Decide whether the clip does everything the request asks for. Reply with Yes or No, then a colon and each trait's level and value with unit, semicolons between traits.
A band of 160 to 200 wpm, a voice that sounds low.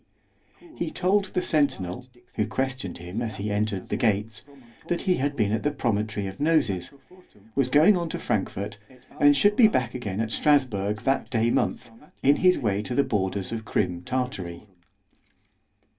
Yes: average, 165 wpm; low, 120 Hz